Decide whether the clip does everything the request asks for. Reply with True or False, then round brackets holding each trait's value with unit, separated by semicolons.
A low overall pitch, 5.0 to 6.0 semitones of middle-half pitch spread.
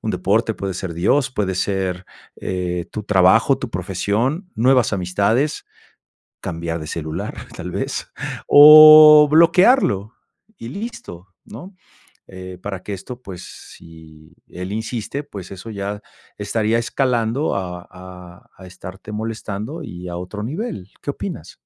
True (100 Hz; 5.6 semitones)